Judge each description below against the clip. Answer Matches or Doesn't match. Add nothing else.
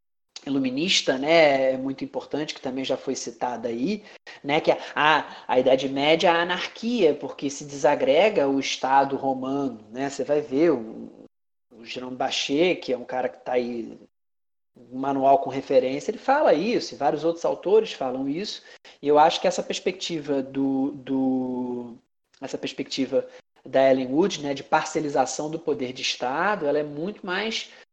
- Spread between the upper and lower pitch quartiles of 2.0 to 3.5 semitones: Doesn't match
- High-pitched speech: Doesn't match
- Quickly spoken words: Doesn't match